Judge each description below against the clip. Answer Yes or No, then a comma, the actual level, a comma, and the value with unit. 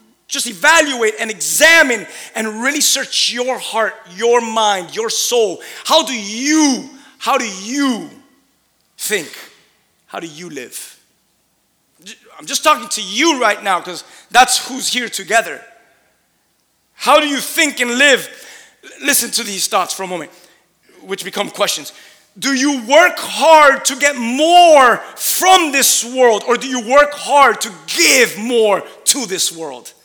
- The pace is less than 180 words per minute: Yes, average, 145 wpm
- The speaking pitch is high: Yes, high, 245 Hz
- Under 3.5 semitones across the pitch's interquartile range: No, average, 4.7 semitones